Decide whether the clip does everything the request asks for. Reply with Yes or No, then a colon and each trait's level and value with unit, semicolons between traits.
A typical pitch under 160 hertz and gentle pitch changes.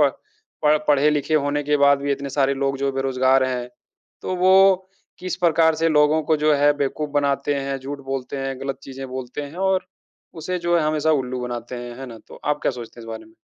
Yes: medium, 140 Hz; narrow, 2.3 semitones